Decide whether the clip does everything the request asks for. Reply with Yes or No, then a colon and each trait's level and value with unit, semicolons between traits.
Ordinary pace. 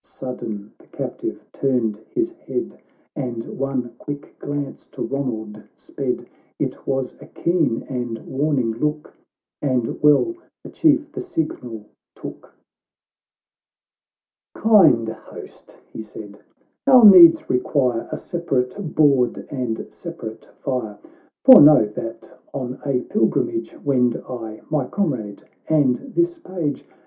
No: slow, 125 wpm